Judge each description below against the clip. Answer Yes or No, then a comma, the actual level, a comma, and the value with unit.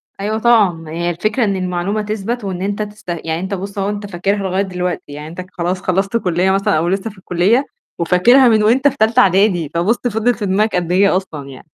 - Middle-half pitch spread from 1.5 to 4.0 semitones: Yes, average, 3.2 semitones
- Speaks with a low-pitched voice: No, high, 195 Hz